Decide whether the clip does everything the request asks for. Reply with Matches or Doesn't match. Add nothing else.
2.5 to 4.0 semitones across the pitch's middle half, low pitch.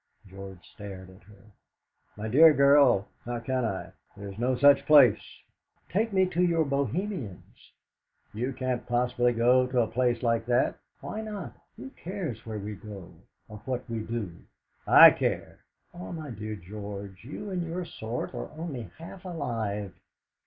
Doesn't match